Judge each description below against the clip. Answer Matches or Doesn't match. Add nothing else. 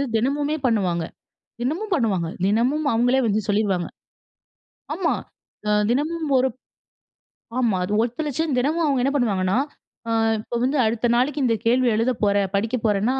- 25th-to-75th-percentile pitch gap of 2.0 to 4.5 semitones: Doesn't match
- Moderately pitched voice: Doesn't match